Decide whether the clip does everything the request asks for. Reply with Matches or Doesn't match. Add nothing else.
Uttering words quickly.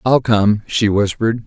Doesn't match